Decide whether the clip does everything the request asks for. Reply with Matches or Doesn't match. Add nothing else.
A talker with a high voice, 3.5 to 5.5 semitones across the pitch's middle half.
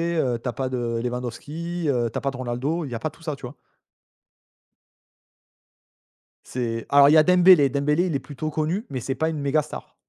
Doesn't match